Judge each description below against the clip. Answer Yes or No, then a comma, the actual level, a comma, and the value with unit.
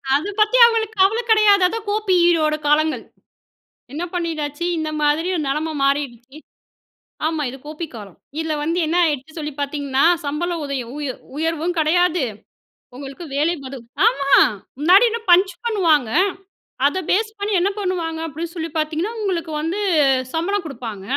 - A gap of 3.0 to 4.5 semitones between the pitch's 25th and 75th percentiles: Yes, average, 3.8 semitones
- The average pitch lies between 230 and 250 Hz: No, very high, 320 Hz